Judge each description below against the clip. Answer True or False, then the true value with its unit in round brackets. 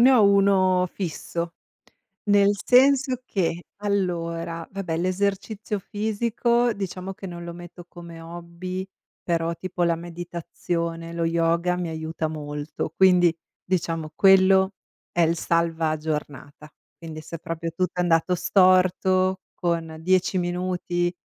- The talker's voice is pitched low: False (175 Hz)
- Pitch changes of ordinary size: False (2.2 semitones)